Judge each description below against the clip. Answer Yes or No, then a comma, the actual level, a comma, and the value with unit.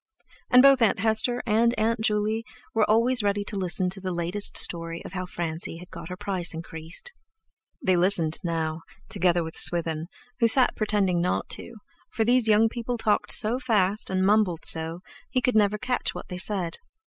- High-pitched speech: Yes, high, 200 Hz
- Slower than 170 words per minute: No, average, 185 wpm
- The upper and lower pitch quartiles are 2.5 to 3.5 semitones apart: No, average, 4.3 semitones